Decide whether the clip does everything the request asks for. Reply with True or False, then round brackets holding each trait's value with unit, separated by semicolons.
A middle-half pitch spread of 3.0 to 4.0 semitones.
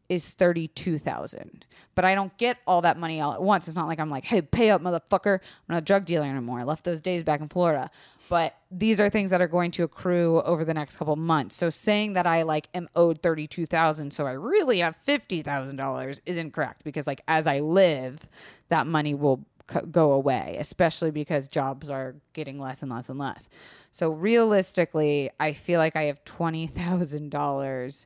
True (3.4 semitones)